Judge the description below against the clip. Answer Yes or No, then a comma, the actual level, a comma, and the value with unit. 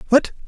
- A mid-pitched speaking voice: No, very high, 270 Hz